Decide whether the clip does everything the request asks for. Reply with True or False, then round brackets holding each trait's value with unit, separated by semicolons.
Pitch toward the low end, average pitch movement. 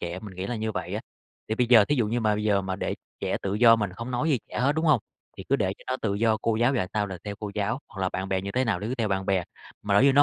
True (110 Hz; 3.6 semitones)